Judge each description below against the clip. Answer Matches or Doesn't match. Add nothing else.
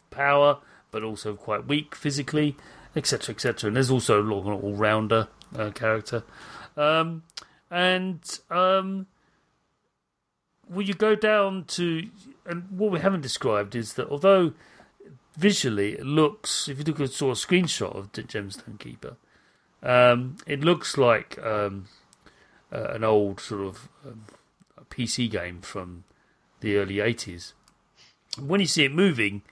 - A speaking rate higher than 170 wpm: Doesn't match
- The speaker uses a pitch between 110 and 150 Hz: Matches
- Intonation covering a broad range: Matches